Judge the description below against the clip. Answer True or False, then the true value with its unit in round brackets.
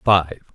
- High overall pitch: False (85 Hz)